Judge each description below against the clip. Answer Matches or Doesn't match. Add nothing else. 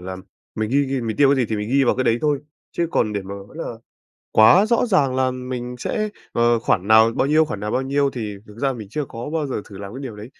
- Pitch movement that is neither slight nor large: Matches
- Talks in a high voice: Doesn't match